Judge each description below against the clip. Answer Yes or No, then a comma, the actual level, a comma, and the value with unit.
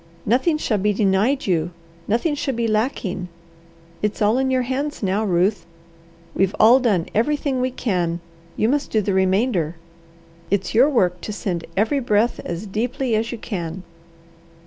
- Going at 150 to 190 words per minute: Yes, average, 160 wpm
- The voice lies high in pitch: Yes, high, 215 Hz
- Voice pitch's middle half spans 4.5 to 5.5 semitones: Yes, average, 4.9 semitones